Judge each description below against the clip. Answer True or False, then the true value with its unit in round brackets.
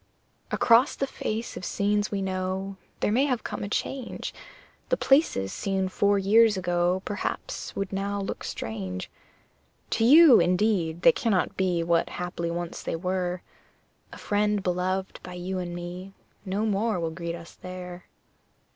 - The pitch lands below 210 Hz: True (190 Hz)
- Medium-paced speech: True (155 wpm)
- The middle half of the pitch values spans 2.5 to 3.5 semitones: True (2.8 semitones)